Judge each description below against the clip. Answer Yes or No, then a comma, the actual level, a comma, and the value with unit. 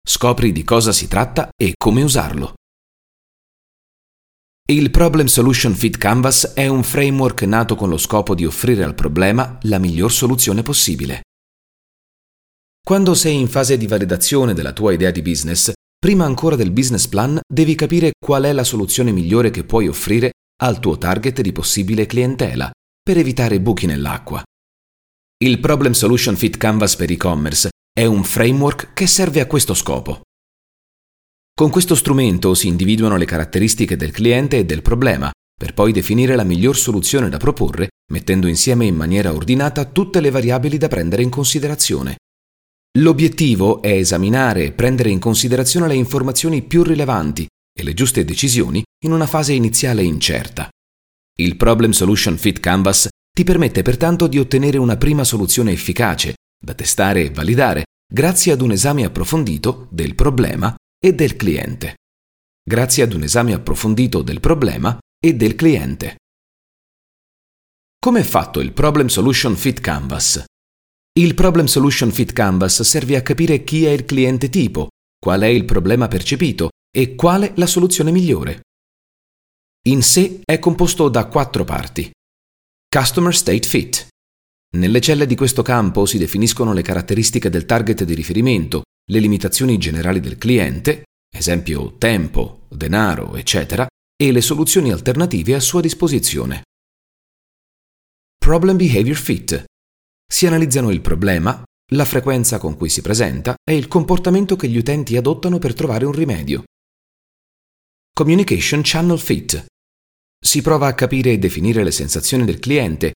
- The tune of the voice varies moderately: No, wide, 7.8 semitones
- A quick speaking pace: No, average, 145 wpm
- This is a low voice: Yes, low, 115 Hz